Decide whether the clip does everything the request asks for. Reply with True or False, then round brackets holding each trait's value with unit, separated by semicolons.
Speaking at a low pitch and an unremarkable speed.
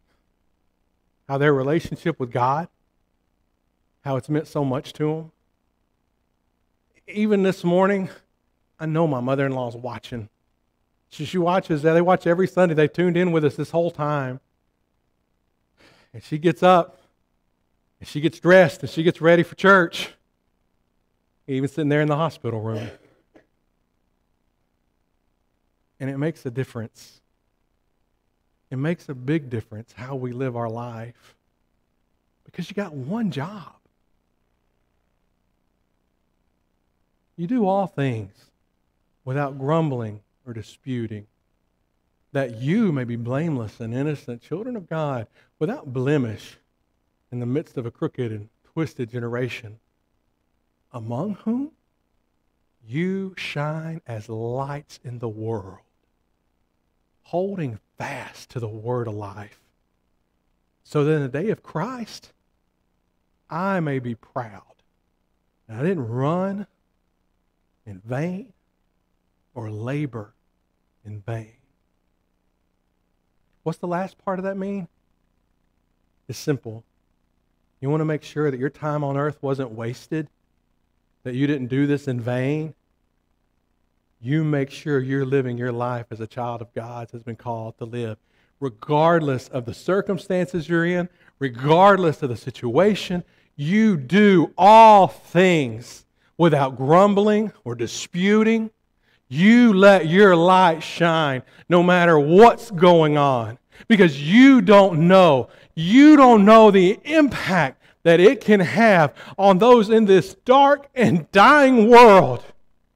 False (130 Hz; 125 wpm)